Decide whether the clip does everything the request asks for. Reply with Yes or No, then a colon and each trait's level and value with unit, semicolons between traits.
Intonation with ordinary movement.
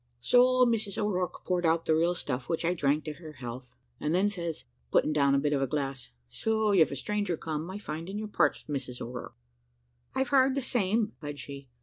No: wide, 6.7 semitones